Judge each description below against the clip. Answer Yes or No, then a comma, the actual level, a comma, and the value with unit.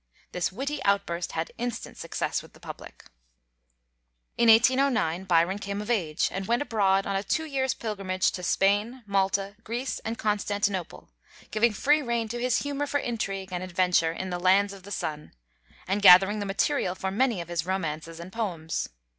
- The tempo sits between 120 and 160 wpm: No, average, 175 wpm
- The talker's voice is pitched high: Yes, high, 200 Hz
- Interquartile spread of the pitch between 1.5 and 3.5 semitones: No, average, 4.0 semitones